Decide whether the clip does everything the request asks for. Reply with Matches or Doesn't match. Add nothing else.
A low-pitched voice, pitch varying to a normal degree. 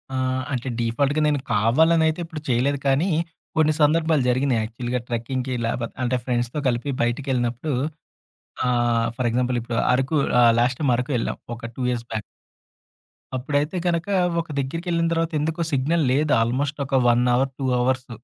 Matches